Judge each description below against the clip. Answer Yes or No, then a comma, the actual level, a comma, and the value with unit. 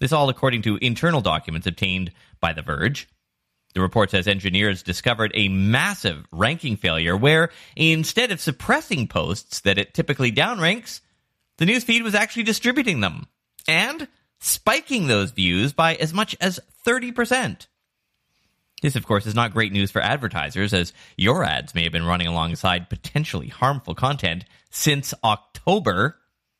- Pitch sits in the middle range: No, low, 120 Hz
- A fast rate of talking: No, average, 145 wpm